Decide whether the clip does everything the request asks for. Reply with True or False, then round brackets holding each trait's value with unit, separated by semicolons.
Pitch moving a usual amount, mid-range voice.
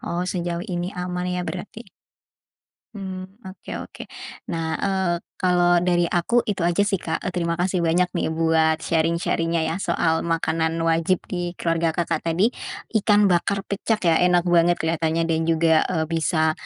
False (1.8 semitones; 175 Hz)